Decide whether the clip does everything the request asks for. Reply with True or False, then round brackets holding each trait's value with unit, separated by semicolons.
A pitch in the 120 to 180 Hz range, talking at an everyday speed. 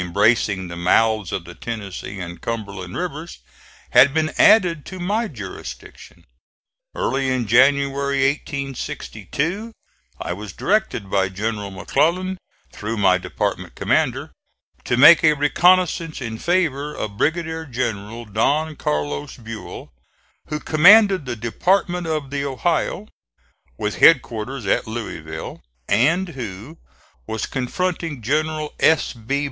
False (135 Hz; 120 wpm)